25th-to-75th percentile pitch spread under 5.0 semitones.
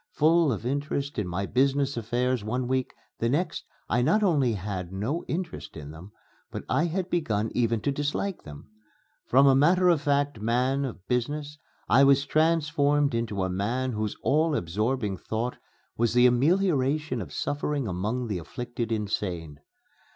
No: average, 5.3 semitones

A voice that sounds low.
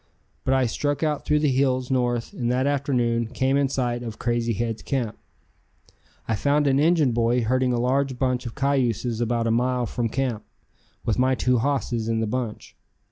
Yes: low, 125 Hz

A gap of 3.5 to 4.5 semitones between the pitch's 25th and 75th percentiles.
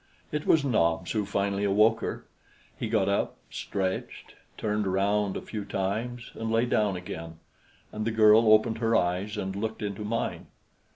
No: narrow, 2.4 semitones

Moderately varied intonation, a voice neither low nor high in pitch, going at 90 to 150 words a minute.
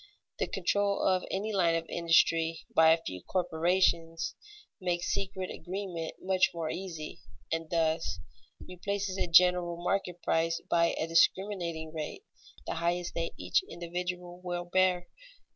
No: narrow, 2.0 semitones; medium, 175 Hz; slow, 135 wpm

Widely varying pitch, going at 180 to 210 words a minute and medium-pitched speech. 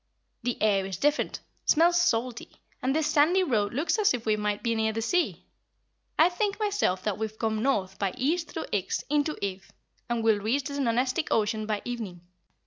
No: wide, 6.2 semitones; average, 185 wpm; high, 235 Hz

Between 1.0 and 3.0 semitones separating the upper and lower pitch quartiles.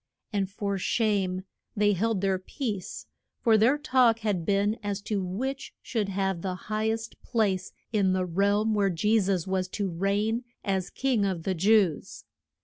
Yes: average, 2.7 semitones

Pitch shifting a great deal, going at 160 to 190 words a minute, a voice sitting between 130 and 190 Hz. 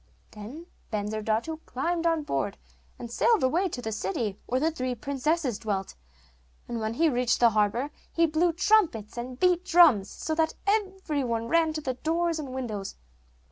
No: wide, 6.4 semitones; average, 170 wpm; very high, 265 Hz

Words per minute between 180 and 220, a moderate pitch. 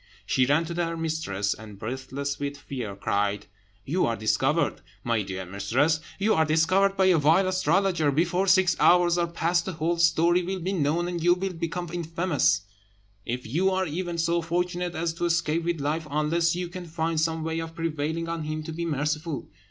Yes: average, 190 wpm; medium, 165 Hz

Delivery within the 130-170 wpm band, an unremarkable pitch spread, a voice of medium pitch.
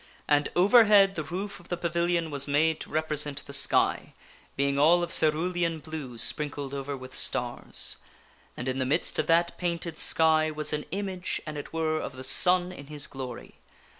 No: average, 180 wpm; average, 3.5 semitones; medium, 155 Hz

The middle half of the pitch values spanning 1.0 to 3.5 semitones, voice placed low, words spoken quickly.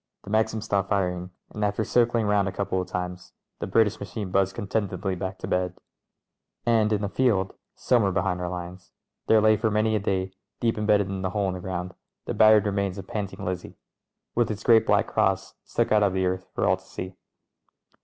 Yes: narrow, 2.6 semitones; low, 100 Hz; fast, 215 wpm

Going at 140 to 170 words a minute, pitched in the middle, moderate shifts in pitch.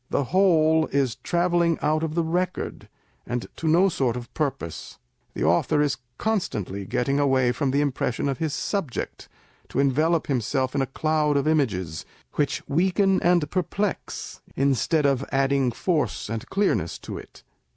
Yes: average, 160 wpm; medium, 145 Hz; average, 4.2 semitones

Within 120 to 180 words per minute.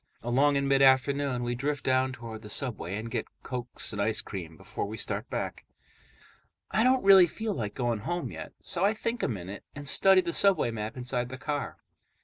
No: average, 200 wpm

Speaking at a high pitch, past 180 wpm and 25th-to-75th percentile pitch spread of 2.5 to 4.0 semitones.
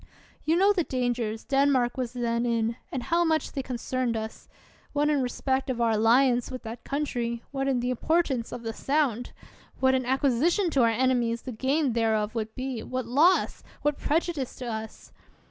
Yes: very high, 255 Hz; average, 190 wpm; average, 3.1 semitones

